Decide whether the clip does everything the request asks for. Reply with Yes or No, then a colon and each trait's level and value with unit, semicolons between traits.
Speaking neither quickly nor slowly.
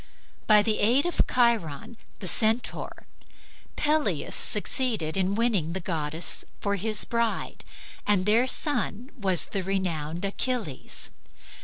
No: slow, 120 wpm